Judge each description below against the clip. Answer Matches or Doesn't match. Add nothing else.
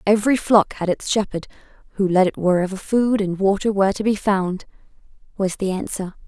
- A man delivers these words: Doesn't match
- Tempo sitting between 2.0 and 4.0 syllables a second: Doesn't match